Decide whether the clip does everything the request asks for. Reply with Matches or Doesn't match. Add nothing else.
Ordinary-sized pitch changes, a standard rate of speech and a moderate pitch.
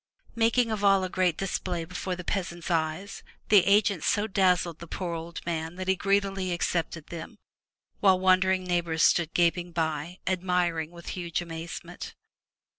Doesn't match